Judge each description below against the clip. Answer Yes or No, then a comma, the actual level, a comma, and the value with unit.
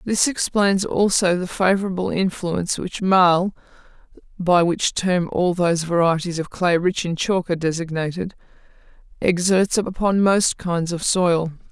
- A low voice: No, medium, 180 Hz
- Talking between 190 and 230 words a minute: No, average, 140 wpm